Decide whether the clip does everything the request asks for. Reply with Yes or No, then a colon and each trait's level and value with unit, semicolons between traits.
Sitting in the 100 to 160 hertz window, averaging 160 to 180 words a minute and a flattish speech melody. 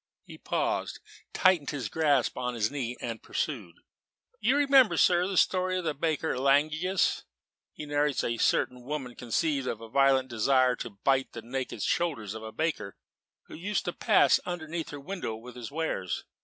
No: medium, 140 Hz; average, 175 wpm; average, 5.2 semitones